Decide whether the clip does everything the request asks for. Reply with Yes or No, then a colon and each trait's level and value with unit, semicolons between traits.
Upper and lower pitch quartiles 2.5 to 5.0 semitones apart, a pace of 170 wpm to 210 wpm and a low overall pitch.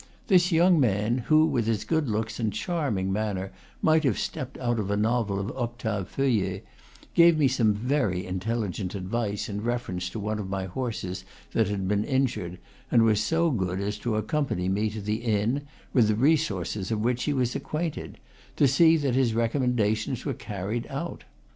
Yes: average, 4.5 semitones; average, 185 wpm; low, 110 Hz